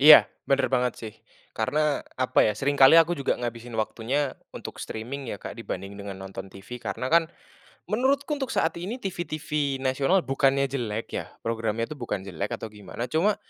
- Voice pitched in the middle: No, low, 130 Hz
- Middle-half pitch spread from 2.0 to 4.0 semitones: No, wide, 5.4 semitones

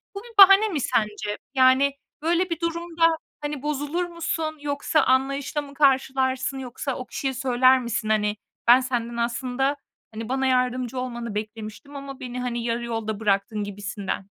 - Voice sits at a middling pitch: No, very high, 260 Hz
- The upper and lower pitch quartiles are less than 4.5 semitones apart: Yes, average, 3.7 semitones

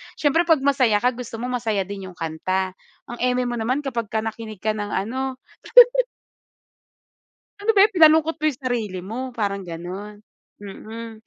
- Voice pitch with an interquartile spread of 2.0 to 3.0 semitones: No, average, 4.3 semitones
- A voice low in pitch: No, high, 230 Hz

